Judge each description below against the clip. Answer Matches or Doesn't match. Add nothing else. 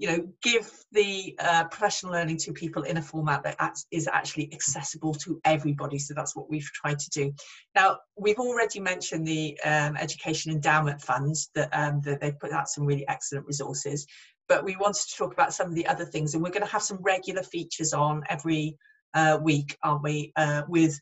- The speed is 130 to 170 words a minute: Doesn't match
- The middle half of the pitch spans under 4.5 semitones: Matches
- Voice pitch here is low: Doesn't match